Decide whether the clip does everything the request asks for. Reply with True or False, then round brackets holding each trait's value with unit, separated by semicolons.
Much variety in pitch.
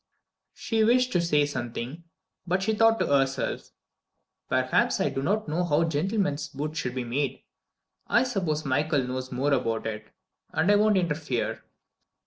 True (6.4 semitones)